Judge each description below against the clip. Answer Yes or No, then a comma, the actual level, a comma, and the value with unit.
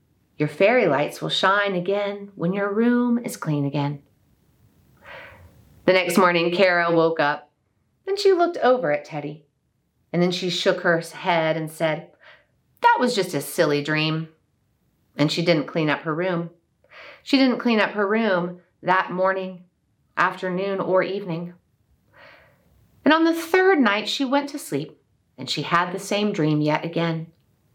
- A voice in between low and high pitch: Yes, medium, 175 Hz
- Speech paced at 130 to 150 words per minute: No, average, 160 wpm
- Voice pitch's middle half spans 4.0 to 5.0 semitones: Yes, average, 4.3 semitones